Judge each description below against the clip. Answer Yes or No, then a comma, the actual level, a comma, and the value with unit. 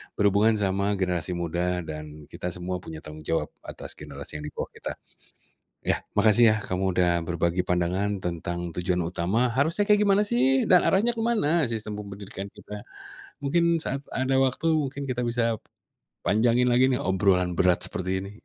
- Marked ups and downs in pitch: Yes, wide, 6.5 semitones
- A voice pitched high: No, low, 100 Hz